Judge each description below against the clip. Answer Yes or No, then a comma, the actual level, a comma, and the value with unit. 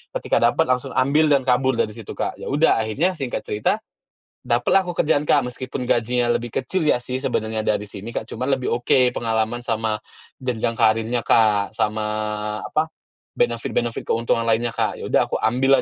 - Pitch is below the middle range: Yes, low, 120 Hz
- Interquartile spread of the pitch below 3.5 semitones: Yes, average, 2.8 semitones